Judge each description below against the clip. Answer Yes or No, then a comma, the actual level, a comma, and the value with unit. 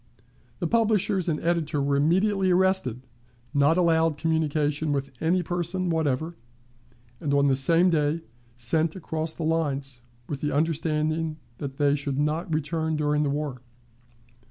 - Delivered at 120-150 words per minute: Yes, average, 140 wpm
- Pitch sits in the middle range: Yes, medium, 155 Hz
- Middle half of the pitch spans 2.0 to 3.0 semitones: Yes, narrow, 2.6 semitones